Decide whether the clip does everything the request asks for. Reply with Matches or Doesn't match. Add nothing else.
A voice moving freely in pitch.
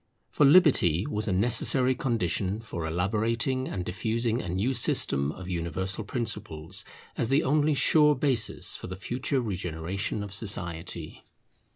Matches